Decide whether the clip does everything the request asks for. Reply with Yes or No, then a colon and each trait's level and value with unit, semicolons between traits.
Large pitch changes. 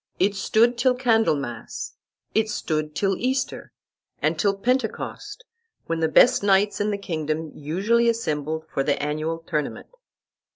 Yes: wide, 6.9 semitones